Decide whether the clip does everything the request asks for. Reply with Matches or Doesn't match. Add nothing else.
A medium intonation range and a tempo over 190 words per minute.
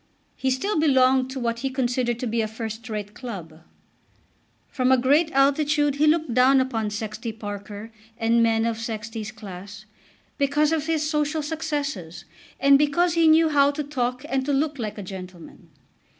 Doesn't match